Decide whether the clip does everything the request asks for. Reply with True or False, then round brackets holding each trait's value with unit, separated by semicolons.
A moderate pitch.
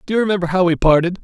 True (180 Hz)